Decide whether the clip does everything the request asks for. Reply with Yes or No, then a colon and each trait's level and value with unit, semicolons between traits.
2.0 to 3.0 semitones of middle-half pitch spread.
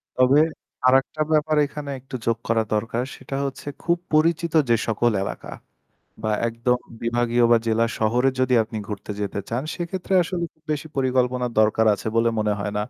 No: average, 4.0 semitones